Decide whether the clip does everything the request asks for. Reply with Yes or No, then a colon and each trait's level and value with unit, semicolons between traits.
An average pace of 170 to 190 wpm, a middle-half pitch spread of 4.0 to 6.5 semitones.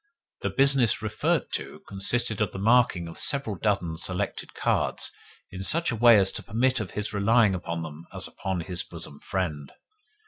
Yes: average, 175 wpm; average, 4.8 semitones